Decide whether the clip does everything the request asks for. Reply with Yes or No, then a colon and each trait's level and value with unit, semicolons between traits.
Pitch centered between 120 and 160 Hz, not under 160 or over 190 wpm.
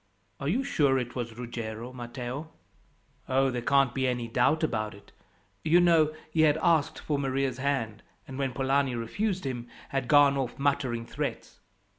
Yes: low, 135 Hz; average, 165 wpm